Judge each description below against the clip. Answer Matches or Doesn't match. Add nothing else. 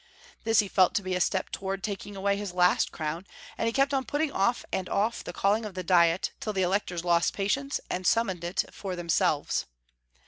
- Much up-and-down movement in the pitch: Doesn't match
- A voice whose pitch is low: Doesn't match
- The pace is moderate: Doesn't match